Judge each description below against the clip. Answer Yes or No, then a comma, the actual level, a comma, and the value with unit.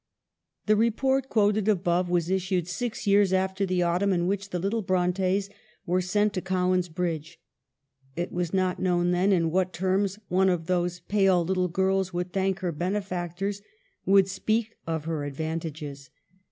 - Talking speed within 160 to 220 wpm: Yes, average, 165 wpm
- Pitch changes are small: Yes, narrow, 2.0 semitones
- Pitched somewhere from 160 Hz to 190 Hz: Yes, medium, 185 Hz